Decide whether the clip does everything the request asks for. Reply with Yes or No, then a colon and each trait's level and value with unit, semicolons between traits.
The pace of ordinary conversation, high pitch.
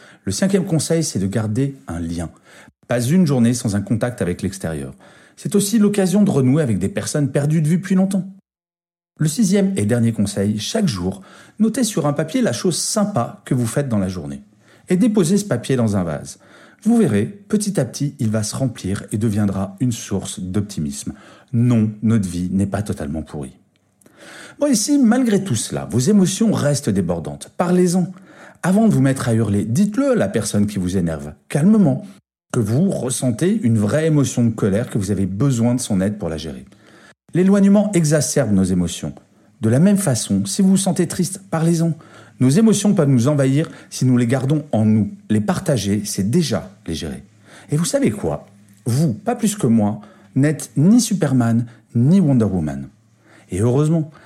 No: average, 185 wpm; low, 130 Hz